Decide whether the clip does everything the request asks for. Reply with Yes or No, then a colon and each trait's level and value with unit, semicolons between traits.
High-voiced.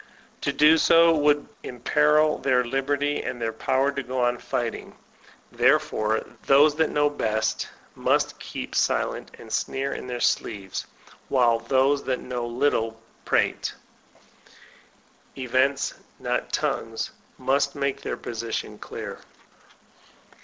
No: low, 135 Hz